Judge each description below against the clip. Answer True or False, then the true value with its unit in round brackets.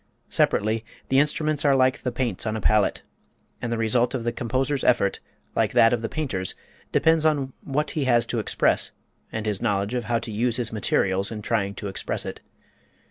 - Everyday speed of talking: True (195 wpm)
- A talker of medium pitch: False (120 Hz)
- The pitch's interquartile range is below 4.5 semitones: True (3.5 semitones)